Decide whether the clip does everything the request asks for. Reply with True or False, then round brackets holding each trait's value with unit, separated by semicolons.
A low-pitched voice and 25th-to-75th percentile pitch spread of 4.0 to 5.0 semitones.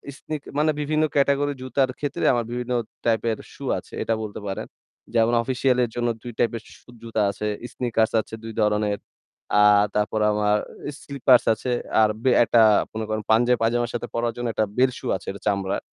False (115 Hz; 2.7 semitones)